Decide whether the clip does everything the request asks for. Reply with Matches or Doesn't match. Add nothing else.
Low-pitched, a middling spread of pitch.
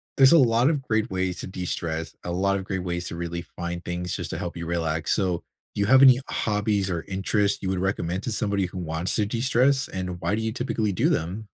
Matches